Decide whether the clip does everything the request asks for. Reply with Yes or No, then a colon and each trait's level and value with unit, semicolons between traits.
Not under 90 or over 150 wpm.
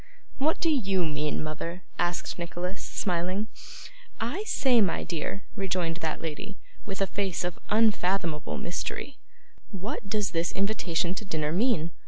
Yes: average, 140 wpm